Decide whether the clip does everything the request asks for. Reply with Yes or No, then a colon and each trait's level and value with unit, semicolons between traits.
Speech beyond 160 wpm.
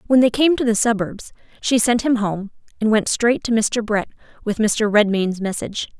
Yes: average, 200 wpm